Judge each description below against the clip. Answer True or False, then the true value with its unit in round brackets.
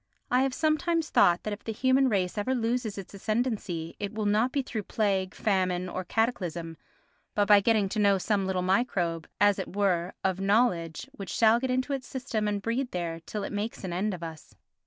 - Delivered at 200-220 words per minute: True (205 wpm)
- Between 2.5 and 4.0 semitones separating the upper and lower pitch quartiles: False (4.4 semitones)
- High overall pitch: True (205 Hz)